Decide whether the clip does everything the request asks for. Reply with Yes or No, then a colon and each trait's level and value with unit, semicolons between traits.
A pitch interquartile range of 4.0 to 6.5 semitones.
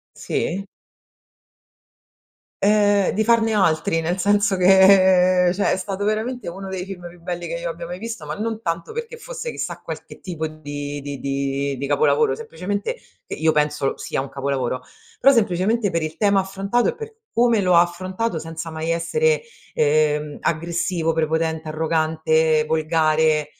Yes: average, 4.3 semitones